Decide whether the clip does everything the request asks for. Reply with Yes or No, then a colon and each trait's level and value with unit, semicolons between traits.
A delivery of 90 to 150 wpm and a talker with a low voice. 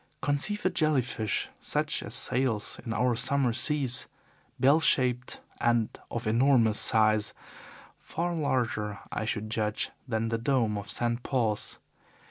Yes: slow, 135 wpm; low, 120 Hz